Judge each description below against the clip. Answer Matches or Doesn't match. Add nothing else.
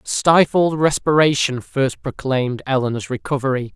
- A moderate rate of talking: Doesn't match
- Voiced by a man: Matches